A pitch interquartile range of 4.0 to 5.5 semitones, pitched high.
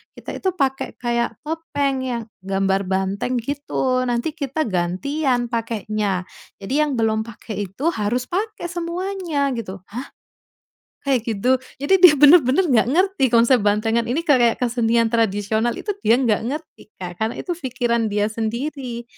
Yes: average, 4.6 semitones; high, 240 Hz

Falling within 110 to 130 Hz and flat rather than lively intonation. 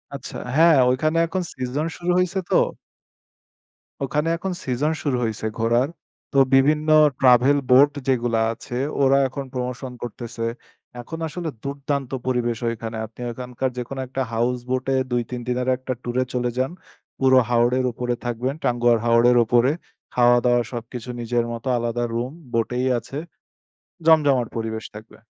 Yes: low, 125 Hz; narrow, 2.3 semitones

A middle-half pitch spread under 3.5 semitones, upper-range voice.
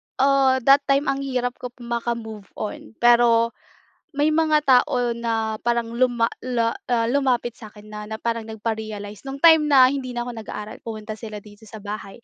Yes: average, 2.8 semitones; high, 235 Hz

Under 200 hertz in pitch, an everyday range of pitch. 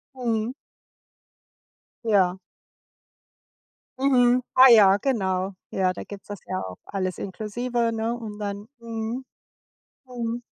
No: high, 220 Hz; average, 3.5 semitones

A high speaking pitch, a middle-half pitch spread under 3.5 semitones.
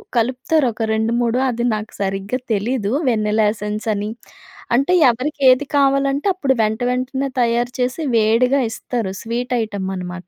Yes: high, 235 Hz; average, 3.1 semitones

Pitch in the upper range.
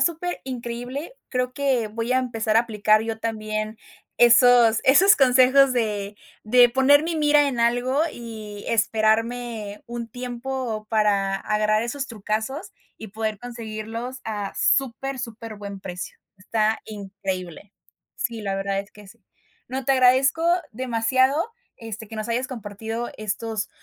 Yes: high, 230 Hz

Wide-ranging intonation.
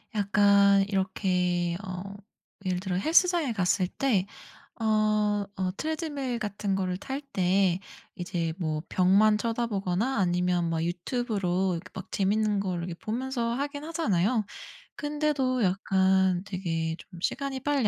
No: average, 4.6 semitones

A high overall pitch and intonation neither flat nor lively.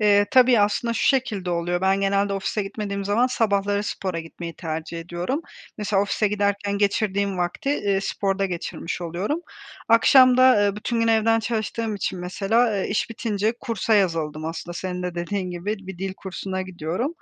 Yes: high, 200 Hz; average, 3.2 semitones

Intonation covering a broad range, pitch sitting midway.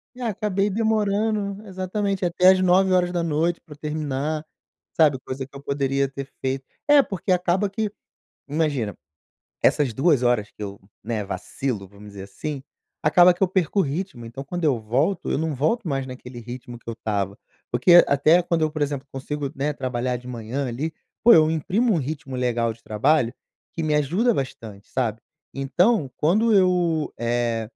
Yes: wide, 6.3 semitones; medium, 150 Hz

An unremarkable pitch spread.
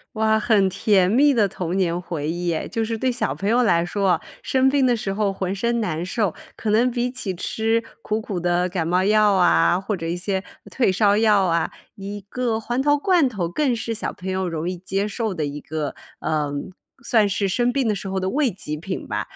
Yes: average, 4.1 semitones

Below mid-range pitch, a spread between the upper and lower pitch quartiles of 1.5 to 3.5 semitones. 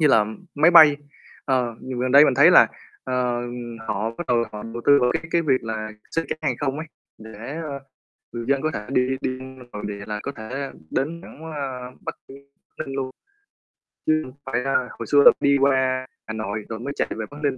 Yes: low, 130 Hz; average, 3.1 semitones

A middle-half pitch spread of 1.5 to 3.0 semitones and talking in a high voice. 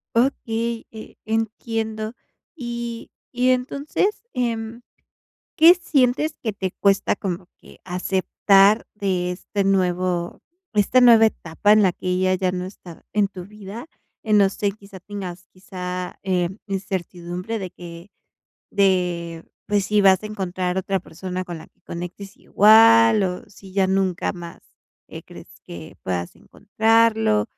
No: average, 3.6 semitones; high, 195 Hz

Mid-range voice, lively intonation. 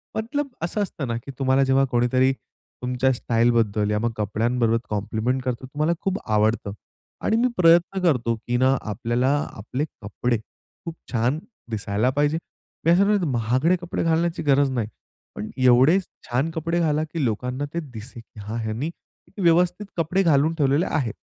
No: low, 130 Hz; wide, 5.8 semitones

